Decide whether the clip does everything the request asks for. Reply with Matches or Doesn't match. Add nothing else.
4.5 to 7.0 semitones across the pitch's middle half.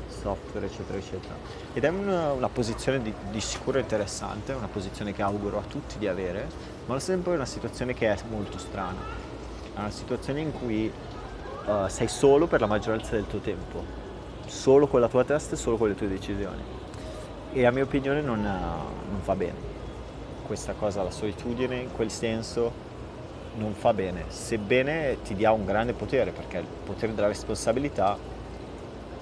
Doesn't match